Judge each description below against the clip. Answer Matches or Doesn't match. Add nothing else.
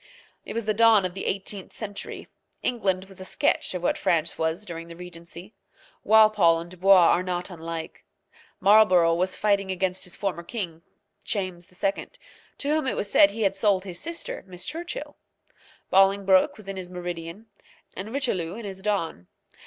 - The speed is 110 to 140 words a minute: Doesn't match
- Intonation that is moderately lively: Matches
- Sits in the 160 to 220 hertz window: Matches